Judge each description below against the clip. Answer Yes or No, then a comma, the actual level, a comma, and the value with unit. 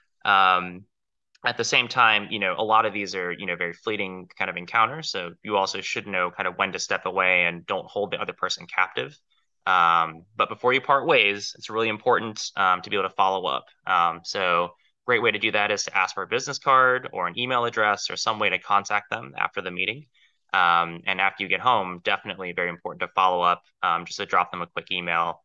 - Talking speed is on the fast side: Yes, fast, 235 wpm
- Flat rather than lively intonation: No, average, 3.7 semitones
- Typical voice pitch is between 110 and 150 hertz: No, very low, 95 Hz